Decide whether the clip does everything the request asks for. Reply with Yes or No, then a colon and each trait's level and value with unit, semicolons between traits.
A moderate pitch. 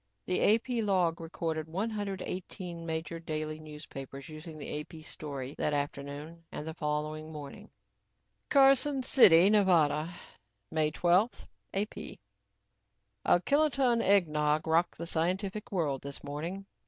Yes: medium, 160 Hz